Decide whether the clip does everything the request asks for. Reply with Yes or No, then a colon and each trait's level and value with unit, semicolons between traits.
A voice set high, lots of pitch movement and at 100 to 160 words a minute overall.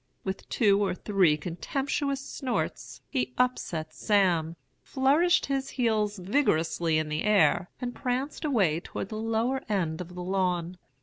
Yes: high, 205 Hz; wide, 6.3 semitones; average, 140 wpm